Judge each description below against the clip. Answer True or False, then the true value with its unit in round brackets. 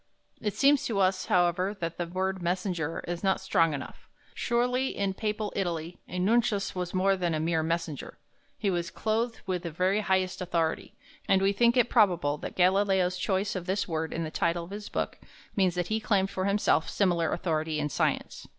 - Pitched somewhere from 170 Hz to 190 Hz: True (185 Hz)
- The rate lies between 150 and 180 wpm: False (195 wpm)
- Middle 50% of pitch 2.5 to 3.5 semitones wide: True (2.9 semitones)